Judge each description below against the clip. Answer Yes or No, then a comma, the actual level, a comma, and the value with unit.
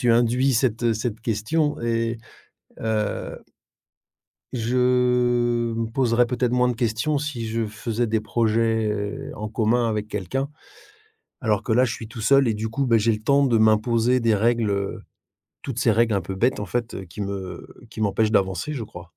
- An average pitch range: No, narrow, 2.3 semitones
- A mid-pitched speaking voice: No, low, 115 Hz